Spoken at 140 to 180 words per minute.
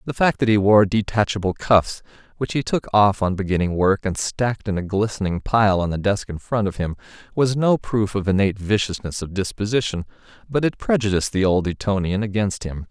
No: average, 200 wpm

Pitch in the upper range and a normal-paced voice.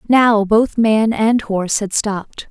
Yes: high, 215 Hz; average, 170 wpm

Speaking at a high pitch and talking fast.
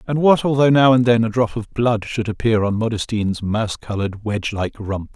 No: low, 115 Hz; fast, 220 wpm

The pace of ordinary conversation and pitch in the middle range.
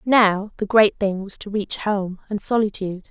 No: average, 195 wpm; high, 205 Hz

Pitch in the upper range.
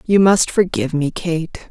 No: medium, 165 Hz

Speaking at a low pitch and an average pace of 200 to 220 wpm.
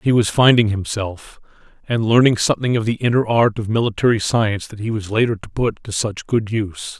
Yes: low, 110 Hz; fast, 205 wpm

